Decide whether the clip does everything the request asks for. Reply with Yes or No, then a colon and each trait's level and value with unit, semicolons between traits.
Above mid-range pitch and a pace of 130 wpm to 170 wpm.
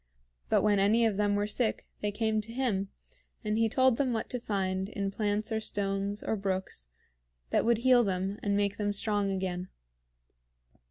No: high, 205 Hz; average, 180 wpm